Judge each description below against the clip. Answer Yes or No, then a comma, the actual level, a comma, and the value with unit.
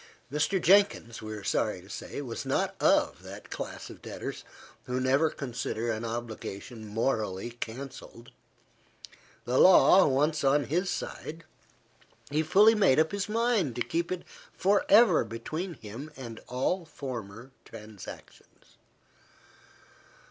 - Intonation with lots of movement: Yes, wide, 6.5 semitones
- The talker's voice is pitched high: No, low, 135 Hz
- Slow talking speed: Yes, slow, 130 wpm